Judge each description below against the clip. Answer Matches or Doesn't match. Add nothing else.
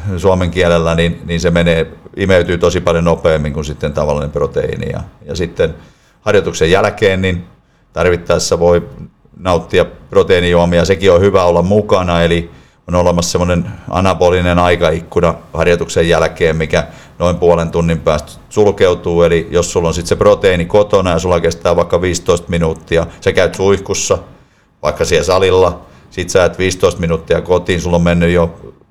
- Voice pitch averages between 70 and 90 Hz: Matches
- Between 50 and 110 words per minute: Doesn't match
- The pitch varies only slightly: Matches